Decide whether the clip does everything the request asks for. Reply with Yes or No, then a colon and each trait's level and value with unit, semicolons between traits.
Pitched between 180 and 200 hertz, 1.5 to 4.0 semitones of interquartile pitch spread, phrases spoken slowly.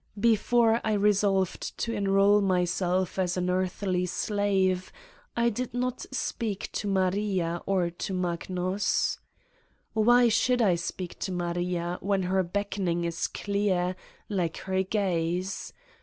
Yes: high, 190 Hz; narrow, 2.5 semitones; slow, 125 wpm